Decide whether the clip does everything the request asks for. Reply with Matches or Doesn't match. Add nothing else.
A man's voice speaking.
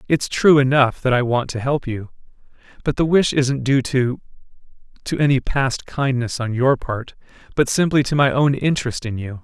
Matches